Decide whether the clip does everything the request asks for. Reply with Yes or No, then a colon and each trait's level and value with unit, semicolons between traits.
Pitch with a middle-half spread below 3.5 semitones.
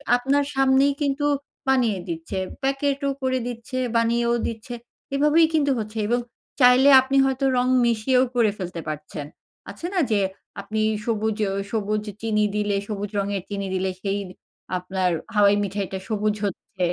No: average, 4.7 semitones